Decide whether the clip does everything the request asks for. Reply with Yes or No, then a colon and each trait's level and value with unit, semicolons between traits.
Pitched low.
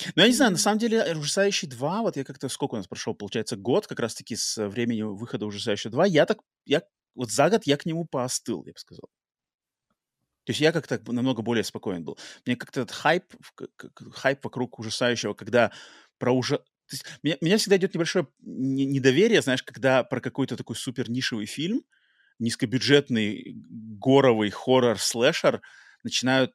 Yes: low, 130 Hz